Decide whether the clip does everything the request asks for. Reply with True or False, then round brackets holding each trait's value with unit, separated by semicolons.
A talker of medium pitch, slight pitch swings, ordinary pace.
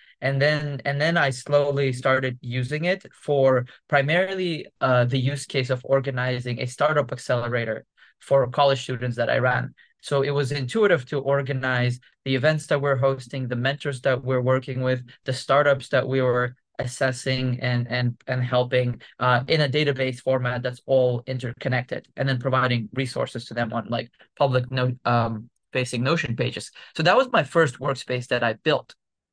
False (130 Hz; 2.1 semitones; 170 wpm)